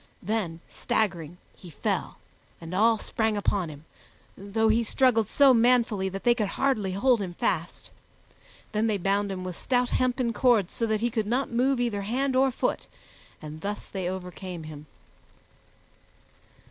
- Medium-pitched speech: No, high, 210 Hz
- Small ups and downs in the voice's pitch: No, average, 4.4 semitones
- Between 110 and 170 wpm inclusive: Yes, average, 160 wpm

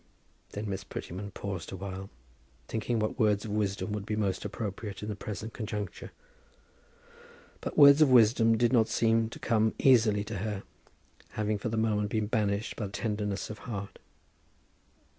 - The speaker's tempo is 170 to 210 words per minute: No, average, 160 wpm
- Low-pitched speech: Yes, low, 105 Hz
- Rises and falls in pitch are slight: Yes, narrow, 1.9 semitones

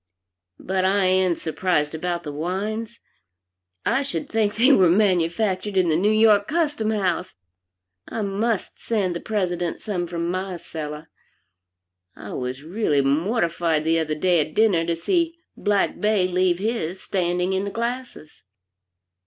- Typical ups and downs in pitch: Yes, average, 4.2 semitones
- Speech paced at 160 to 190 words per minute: No, average, 145 wpm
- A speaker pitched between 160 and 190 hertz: Yes, medium, 185 Hz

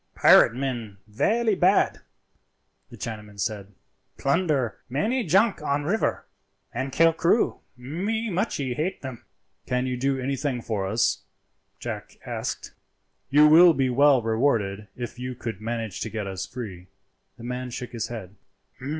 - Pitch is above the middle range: No, low, 125 Hz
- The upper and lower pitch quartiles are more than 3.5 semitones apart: Yes, average, 5.2 semitones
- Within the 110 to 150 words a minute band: Yes, average, 140 wpm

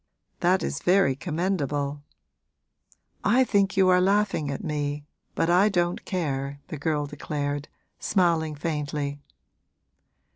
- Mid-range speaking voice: Yes, medium, 155 Hz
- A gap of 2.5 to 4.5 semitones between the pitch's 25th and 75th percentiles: Yes, average, 4.2 semitones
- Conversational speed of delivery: No, slow, 115 wpm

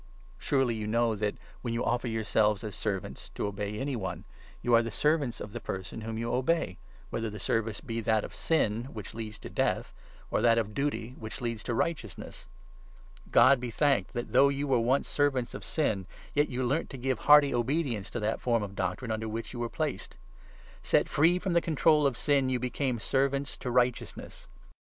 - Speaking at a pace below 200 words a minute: No, fast, 205 wpm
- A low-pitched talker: Yes, low, 120 Hz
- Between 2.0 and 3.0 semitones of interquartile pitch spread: No, average, 3.9 semitones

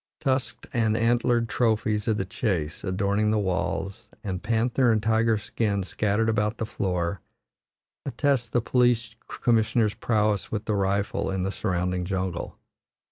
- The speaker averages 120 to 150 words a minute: Yes, average, 140 wpm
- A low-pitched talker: Yes, low, 105 Hz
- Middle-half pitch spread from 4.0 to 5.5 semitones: No, average, 3.1 semitones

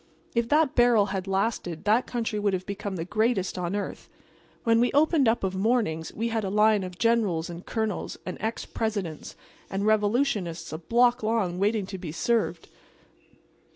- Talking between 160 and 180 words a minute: Yes, average, 175 wpm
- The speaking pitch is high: Yes, high, 210 Hz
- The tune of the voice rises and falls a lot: No, average, 3.7 semitones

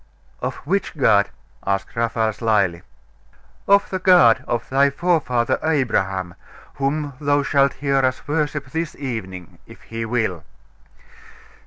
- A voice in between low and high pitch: No, low, 130 Hz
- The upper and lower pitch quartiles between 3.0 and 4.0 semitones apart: No, average, 5.0 semitones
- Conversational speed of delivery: No, slow, 125 wpm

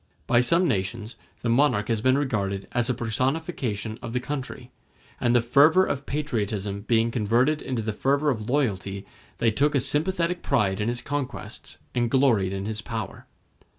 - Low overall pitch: Yes, low, 120 Hz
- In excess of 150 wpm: Yes, average, 170 wpm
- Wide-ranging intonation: No, average, 4.5 semitones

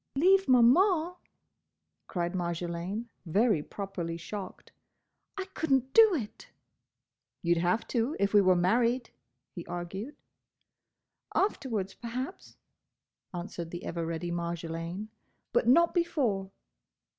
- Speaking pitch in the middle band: No, high, 200 Hz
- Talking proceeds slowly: Yes, slow, 110 wpm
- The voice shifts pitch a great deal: Yes, wide, 7.0 semitones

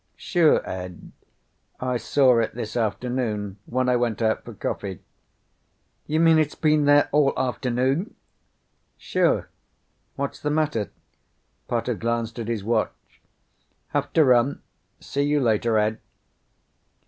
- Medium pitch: No, low, 125 Hz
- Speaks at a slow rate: Yes, slow, 125 wpm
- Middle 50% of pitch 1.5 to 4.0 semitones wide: No, average, 4.6 semitones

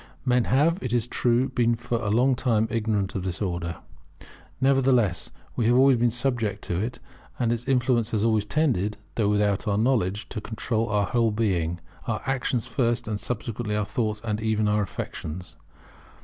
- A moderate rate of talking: Yes, average, 175 wpm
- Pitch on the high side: No, low, 115 Hz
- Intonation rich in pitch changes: No, average, 2.9 semitones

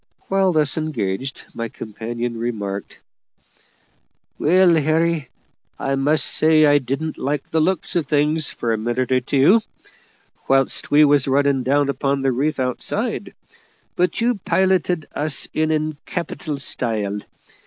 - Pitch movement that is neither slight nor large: Yes, average, 3.7 semitones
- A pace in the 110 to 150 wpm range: Yes, slow, 135 wpm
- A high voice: No, medium, 145 Hz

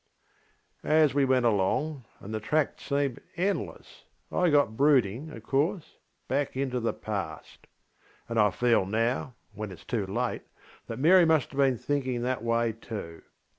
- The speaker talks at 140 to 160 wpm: Yes, average, 150 wpm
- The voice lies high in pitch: No, low, 125 Hz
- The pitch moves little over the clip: No, average, 4.7 semitones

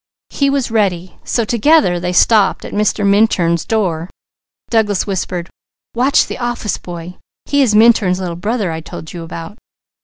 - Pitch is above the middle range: Yes, high, 205 Hz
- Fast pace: No, average, 155 wpm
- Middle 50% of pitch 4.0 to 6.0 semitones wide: Yes, average, 4.6 semitones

